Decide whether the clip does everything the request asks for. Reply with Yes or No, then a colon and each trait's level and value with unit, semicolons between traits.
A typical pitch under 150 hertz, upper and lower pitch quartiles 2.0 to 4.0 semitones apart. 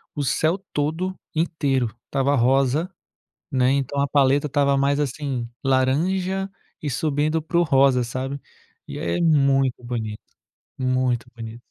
Yes: medium, 140 Hz; average, 2.8 semitones